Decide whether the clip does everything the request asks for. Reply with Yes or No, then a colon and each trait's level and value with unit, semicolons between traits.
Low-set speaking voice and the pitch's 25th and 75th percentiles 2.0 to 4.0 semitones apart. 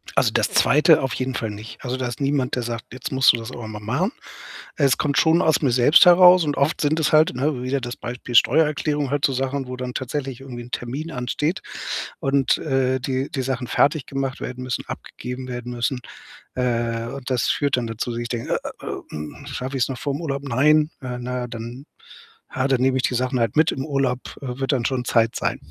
Yes: low, 130 Hz; narrow, 2.4 semitones